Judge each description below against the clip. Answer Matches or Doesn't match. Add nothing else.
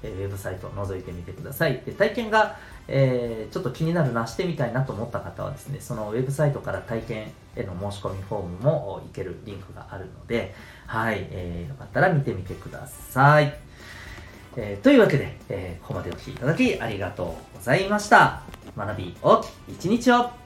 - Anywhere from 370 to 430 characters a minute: Matches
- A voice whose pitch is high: Doesn't match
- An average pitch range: Doesn't match